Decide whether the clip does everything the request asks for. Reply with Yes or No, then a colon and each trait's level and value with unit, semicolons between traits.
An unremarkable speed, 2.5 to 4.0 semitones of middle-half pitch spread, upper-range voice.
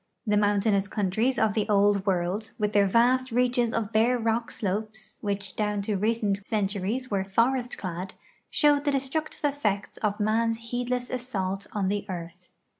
Yes: average, 160 wpm; average, 3.3 semitones; high, 215 Hz